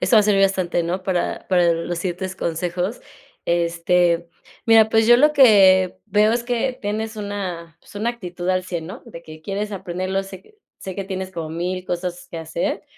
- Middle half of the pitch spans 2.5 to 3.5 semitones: Yes, average, 3.2 semitones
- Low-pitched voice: No, medium, 185 Hz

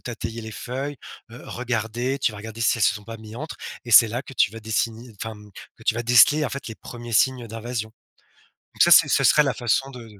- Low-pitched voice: Yes, low, 115 Hz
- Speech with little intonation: Yes, narrow, 2.1 semitones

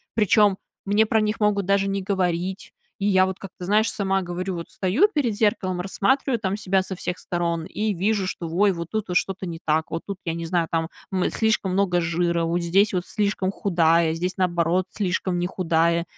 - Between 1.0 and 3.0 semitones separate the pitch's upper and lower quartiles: Yes, average, 2.7 semitones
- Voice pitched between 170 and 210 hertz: Yes, medium, 185 Hz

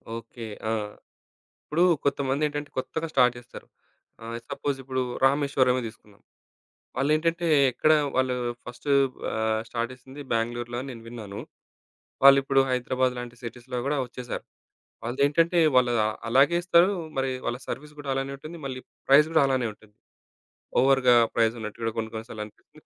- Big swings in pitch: No, average, 2.9 semitones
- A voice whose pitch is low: Yes, low, 130 Hz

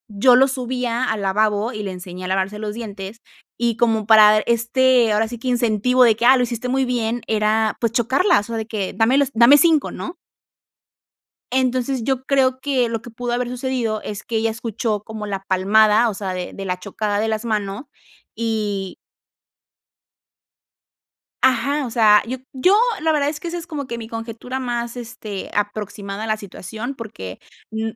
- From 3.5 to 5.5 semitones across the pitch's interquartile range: No, average, 3.1 semitones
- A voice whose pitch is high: Yes, high, 225 Hz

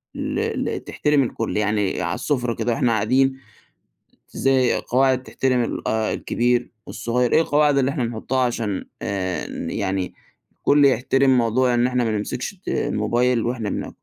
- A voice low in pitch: Yes, low, 125 Hz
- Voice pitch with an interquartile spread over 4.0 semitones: No, average, 3.0 semitones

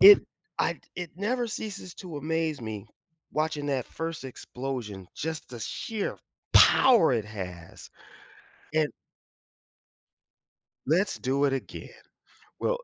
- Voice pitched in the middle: Yes, medium, 150 Hz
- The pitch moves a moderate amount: No, wide, 6.4 semitones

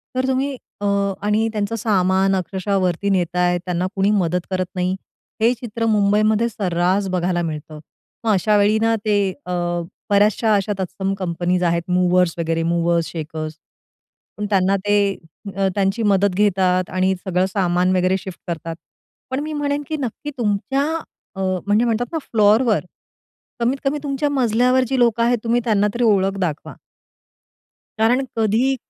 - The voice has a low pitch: No, high, 200 Hz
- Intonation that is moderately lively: Yes, average, 3.8 semitones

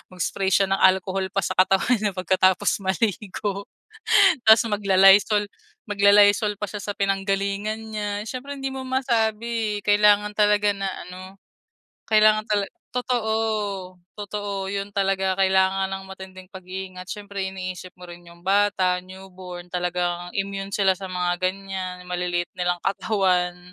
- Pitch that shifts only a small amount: Yes, narrow, 1.8 semitones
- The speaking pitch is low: No, high, 195 Hz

